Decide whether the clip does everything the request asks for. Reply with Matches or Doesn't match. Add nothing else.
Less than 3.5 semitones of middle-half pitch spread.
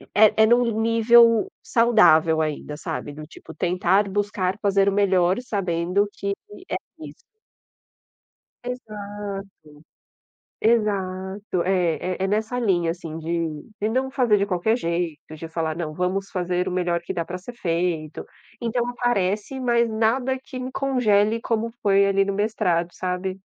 Doesn't match